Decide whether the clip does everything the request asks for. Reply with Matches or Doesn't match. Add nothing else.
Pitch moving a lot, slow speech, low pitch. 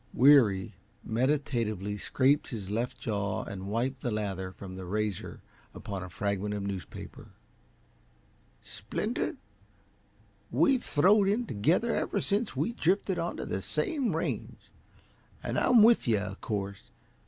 Matches